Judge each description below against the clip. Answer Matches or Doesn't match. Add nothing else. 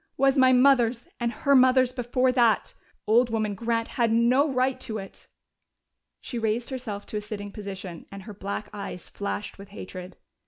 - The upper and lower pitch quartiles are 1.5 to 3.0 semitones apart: Doesn't match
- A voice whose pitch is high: Matches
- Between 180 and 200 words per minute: Doesn't match